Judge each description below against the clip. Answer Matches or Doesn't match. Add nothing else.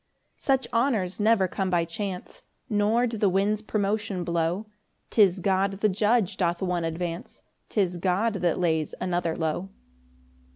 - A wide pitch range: Doesn't match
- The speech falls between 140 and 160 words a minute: Matches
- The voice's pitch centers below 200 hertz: Matches